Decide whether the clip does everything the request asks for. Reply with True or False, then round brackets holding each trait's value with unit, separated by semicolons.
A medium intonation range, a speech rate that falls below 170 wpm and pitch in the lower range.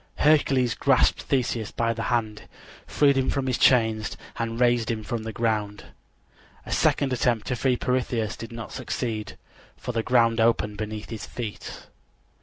False (2.3 semitones; 160 wpm; 115 Hz)